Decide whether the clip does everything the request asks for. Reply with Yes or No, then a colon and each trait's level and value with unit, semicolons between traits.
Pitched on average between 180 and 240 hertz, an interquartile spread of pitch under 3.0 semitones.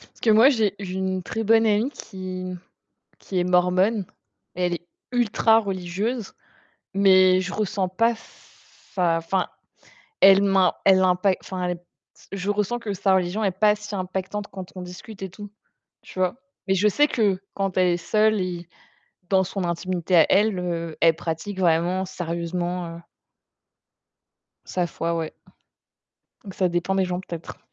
Yes: medium, 185 Hz; narrow, 2.4 semitones